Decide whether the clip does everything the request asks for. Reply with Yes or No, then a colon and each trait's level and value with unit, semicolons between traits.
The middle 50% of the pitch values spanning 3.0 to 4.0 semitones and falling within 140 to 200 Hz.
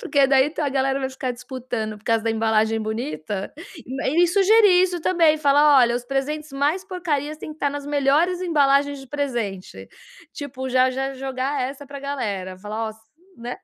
No: average, 3.4 semitones; very high, 270 Hz